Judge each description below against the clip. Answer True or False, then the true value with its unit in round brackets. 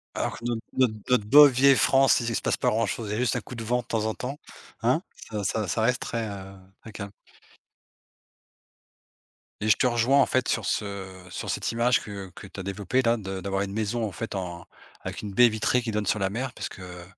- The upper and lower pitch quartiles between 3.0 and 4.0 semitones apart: True (3.5 semitones)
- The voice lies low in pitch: True (110 Hz)